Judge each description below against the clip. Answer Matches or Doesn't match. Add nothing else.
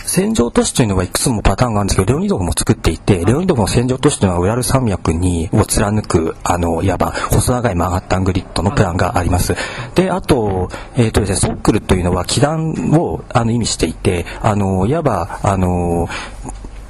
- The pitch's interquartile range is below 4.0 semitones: Doesn't match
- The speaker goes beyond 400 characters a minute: Matches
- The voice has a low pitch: Matches